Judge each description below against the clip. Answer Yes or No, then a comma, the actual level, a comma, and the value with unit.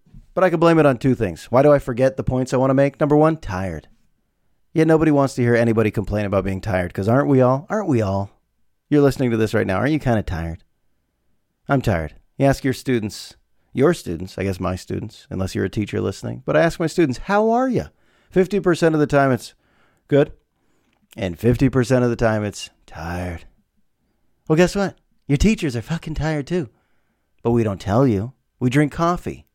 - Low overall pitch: Yes, low, 125 Hz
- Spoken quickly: Yes, fast, 215 wpm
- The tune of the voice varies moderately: No, wide, 7.0 semitones